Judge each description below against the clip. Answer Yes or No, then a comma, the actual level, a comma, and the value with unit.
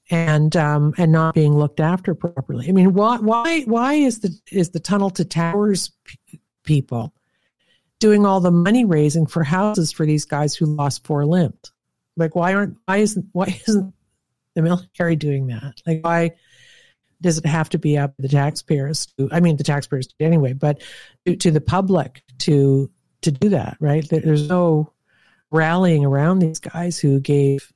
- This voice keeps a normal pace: Yes, average, 180 wpm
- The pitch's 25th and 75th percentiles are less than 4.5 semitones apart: Yes, average, 3.9 semitones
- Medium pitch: Yes, medium, 165 Hz